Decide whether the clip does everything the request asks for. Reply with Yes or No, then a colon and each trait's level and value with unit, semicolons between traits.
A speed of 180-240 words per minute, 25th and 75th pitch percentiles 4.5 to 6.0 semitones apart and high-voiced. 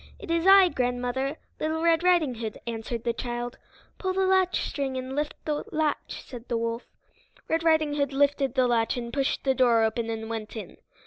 Yes: average, 190 wpm; average, 5.0 semitones; very high, 265 Hz